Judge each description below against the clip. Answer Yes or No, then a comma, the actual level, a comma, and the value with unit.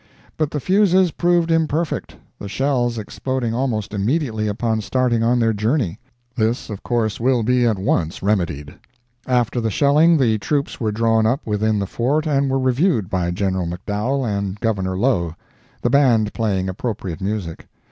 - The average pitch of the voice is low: Yes, low, 115 Hz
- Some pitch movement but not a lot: Yes, average, 4.7 semitones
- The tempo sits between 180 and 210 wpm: No, average, 160 wpm